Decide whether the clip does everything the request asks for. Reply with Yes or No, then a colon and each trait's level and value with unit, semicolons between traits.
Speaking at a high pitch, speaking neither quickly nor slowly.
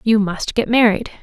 Yes: high, 215 Hz; average, 195 wpm